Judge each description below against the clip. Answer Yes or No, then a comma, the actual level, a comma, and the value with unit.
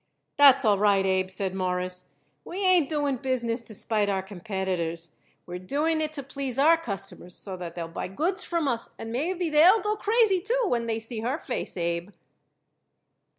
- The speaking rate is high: No, average, 180 wpm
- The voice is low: No, high, 230 Hz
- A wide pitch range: Yes, wide, 8.5 semitones